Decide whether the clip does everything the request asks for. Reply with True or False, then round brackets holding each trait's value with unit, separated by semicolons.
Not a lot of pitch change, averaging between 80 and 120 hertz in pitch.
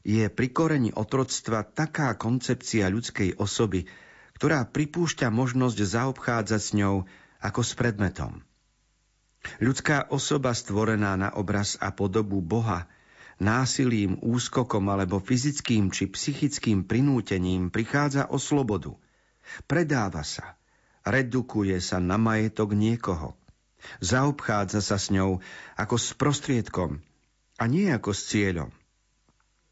False (4.6 semitones; 110 Hz)